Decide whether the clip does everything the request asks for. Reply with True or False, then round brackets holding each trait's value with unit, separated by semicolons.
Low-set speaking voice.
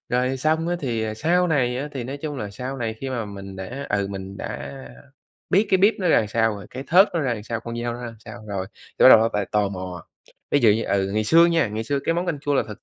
True (120 Hz)